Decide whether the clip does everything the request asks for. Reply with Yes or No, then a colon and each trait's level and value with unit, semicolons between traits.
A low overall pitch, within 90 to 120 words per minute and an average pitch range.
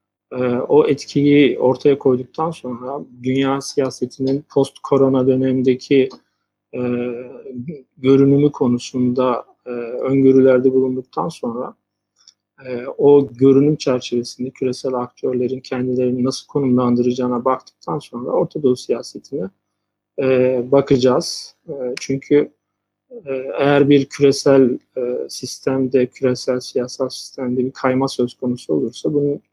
No: low, 130 Hz; average, 100 wpm; narrow, 1.5 semitones